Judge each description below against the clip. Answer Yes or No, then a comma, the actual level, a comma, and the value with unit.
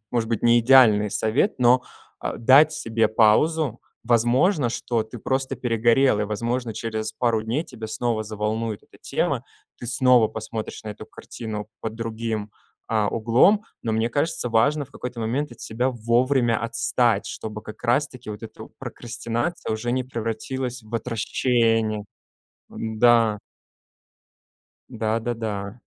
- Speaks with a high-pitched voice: No, low, 115 Hz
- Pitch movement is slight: Yes, narrow, 2.3 semitones